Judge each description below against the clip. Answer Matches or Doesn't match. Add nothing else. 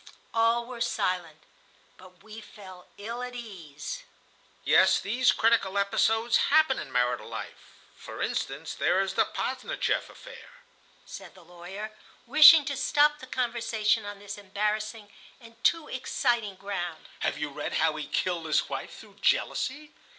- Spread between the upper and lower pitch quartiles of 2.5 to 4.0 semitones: Doesn't match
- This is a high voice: Matches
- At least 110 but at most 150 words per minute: Matches